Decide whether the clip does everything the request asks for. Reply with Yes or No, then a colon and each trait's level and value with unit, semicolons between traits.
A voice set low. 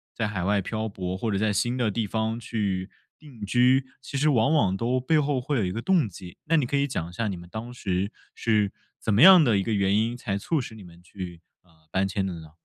Yes: low, 110 Hz